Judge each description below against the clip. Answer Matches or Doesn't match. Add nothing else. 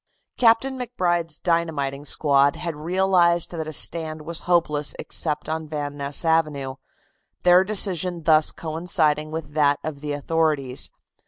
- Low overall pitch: Doesn't match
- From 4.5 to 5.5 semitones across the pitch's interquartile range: Doesn't match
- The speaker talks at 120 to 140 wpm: Matches